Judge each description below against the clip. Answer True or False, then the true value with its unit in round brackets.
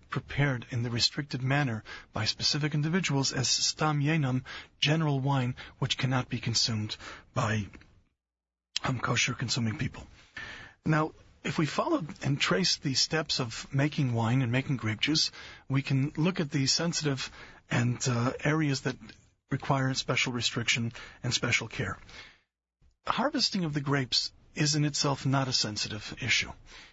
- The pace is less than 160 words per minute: True (145 wpm)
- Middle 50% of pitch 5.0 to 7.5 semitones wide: False (3.9 semitones)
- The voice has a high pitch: False (135 Hz)